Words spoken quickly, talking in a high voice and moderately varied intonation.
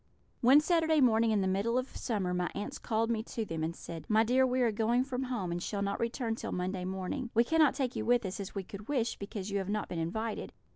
Yes: fast, 255 wpm; high, 220 Hz; average, 4.4 semitones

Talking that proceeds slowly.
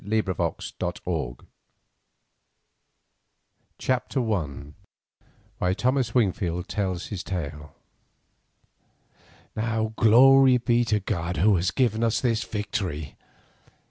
Yes: slow, 90 wpm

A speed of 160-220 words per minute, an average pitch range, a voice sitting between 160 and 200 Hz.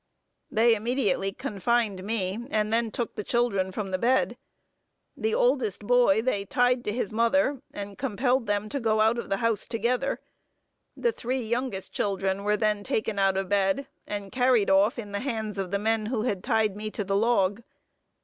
No: average, 185 wpm; average, 3.3 semitones; high, 215 Hz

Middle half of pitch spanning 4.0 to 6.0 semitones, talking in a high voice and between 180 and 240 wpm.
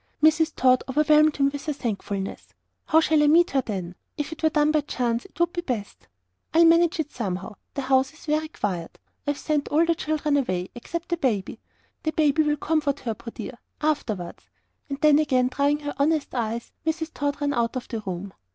Yes: average, 4.7 semitones; very high, 285 Hz; average, 195 wpm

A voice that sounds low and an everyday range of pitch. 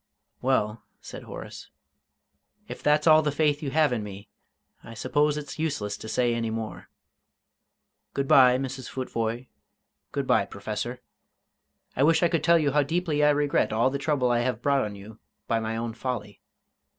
Yes: low, 130 Hz; average, 4.5 semitones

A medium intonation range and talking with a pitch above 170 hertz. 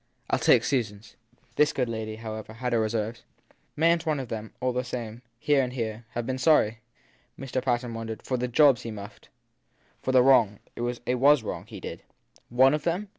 No: average, 3.1 semitones; low, 120 Hz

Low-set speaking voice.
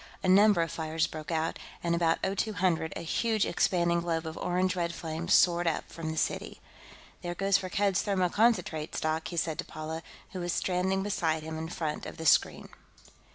No: medium, 170 Hz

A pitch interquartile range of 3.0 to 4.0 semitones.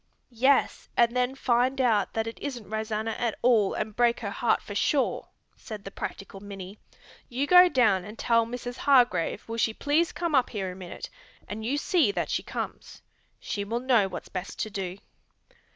Yes: average, 3.6 semitones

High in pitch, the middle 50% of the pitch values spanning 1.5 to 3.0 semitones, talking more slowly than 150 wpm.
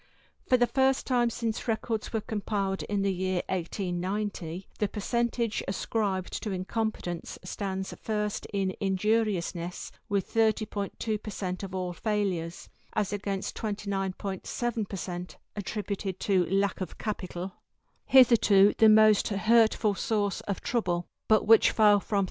Yes: high, 205 Hz; narrow, 2.5 semitones; slow, 135 wpm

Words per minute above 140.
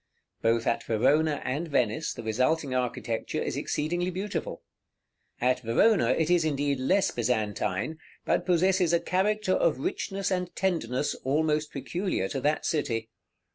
No: slow, 135 wpm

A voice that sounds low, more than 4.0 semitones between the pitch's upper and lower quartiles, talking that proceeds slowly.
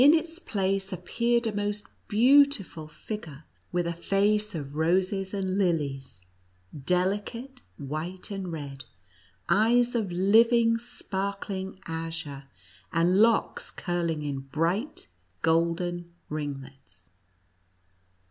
No: medium, 185 Hz; average, 4.7 semitones; slow, 100 wpm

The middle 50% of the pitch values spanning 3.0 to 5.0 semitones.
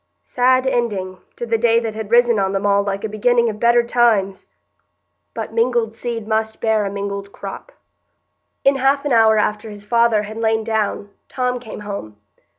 No: narrow, 2.6 semitones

